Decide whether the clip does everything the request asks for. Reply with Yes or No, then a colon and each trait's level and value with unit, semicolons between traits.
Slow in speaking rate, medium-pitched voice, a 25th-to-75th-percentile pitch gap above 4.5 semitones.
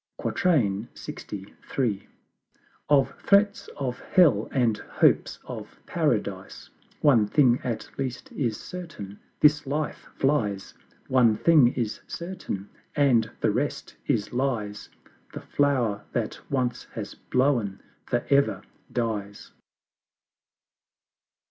No: slow, 100 wpm; low, 125 Hz; average, 5.1 semitones